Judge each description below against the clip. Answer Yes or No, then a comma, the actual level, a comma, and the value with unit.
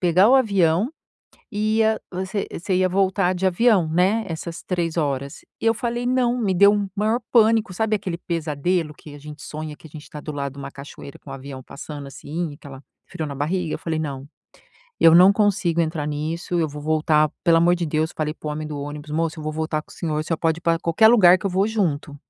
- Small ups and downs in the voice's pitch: No, average, 4.3 semitones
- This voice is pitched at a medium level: Yes, medium, 165 Hz